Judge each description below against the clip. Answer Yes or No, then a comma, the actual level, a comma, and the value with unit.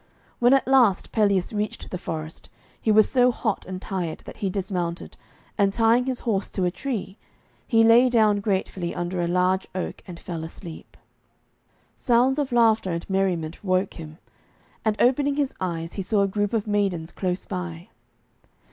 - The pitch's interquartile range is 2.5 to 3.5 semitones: No, average, 4.2 semitones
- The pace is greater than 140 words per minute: Yes, average, 170 wpm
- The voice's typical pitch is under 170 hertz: No, high, 195 Hz